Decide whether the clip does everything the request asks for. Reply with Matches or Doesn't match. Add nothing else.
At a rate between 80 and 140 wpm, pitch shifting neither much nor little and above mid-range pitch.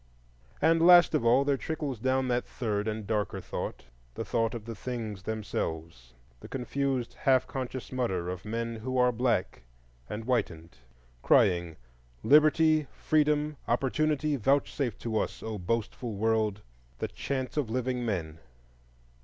Doesn't match